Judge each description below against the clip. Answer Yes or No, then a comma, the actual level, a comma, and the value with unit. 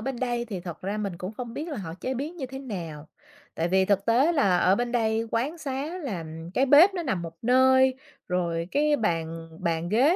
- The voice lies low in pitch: No, high, 230 Hz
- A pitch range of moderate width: No, wide, 6.9 semitones